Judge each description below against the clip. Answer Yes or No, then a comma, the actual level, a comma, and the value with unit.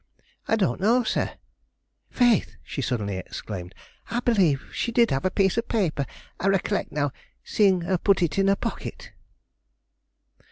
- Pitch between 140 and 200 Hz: Yes, high, 190 Hz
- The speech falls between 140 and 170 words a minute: Yes, average, 155 wpm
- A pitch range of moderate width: No, wide, 7.4 semitones